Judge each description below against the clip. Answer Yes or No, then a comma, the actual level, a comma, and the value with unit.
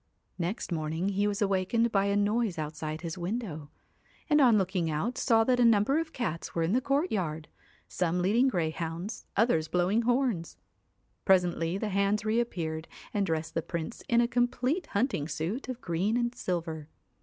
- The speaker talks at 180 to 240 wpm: No, average, 165 wpm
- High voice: Yes, high, 195 Hz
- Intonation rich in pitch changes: Yes, wide, 6.0 semitones